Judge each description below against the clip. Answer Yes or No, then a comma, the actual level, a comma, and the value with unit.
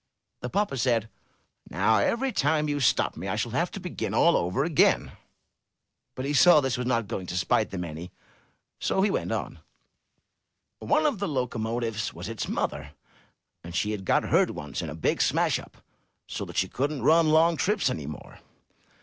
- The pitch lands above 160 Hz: No, low, 125 Hz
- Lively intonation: Yes, wide, 7.9 semitones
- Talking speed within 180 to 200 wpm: Yes, average, 190 wpm